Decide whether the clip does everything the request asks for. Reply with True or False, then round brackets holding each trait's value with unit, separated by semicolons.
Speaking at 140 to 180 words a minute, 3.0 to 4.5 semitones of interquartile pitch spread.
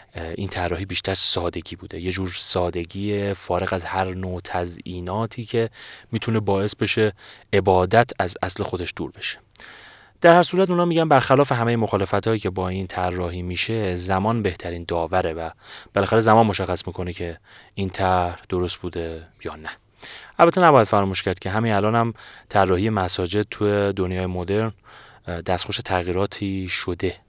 True (145 wpm; 3.3 semitones)